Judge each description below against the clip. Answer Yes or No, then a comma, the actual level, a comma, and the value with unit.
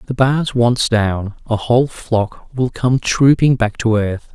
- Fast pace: No, average, 180 wpm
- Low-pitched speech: Yes, low, 120 Hz